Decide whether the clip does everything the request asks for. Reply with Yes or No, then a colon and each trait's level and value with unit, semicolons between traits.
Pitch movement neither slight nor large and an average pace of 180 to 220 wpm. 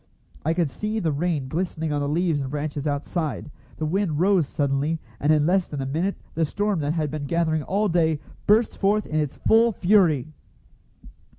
Yes: average, 4.1 semitones; average, 190 wpm